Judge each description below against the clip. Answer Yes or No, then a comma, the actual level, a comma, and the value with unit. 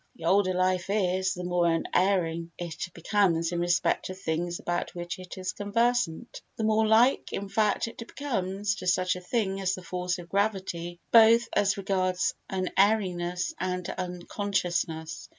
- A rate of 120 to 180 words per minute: Yes, average, 150 wpm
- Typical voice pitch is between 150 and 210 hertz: Yes, medium, 185 Hz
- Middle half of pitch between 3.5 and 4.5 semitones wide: No, narrow, 2.6 semitones